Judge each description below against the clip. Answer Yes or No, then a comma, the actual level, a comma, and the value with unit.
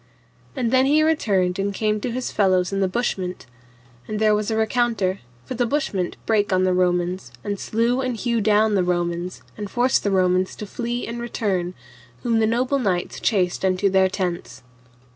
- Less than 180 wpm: No, average, 185 wpm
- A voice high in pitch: Yes, high, 205 Hz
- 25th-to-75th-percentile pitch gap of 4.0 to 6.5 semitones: Yes, average, 4.3 semitones